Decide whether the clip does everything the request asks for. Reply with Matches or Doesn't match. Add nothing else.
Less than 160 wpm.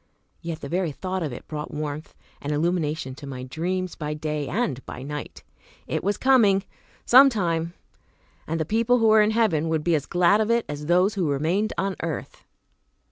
Doesn't match